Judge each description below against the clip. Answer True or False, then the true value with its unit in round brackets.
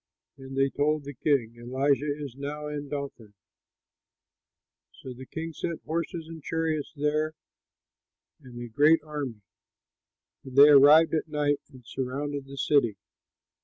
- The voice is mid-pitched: True (145 Hz)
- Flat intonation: True (2.3 semitones)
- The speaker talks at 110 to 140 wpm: True (135 wpm)